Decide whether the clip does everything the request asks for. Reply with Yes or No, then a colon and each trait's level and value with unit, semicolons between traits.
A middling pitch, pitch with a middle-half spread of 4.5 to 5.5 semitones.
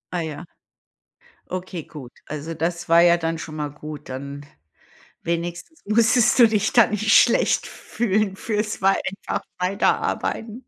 Yes: medium, 175 Hz; average, 5.1 semitones